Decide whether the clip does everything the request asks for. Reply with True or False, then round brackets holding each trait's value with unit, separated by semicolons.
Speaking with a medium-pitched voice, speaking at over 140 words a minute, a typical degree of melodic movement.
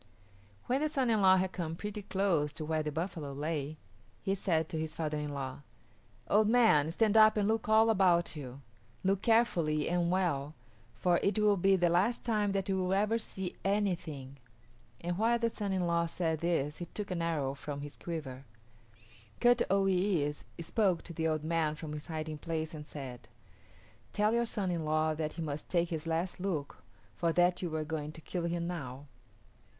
True (170 Hz; 195 wpm; 4.2 semitones)